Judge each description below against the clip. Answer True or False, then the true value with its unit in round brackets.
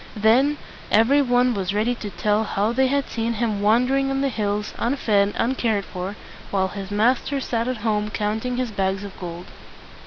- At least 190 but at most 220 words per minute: True (195 wpm)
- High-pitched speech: True (220 Hz)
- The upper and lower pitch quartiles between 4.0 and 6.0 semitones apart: False (3.5 semitones)